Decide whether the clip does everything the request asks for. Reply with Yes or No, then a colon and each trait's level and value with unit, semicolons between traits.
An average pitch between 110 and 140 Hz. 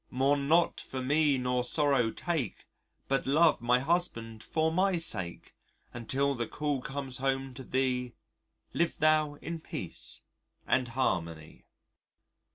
Yes: low, 135 Hz